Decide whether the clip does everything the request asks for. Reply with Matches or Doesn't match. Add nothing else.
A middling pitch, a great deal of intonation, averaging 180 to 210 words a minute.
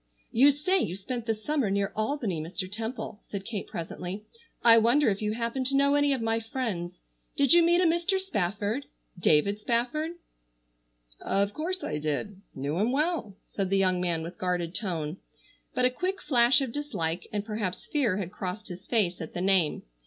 Doesn't match